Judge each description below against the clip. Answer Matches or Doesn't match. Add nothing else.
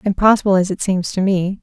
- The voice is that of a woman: Matches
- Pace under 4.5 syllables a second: Doesn't match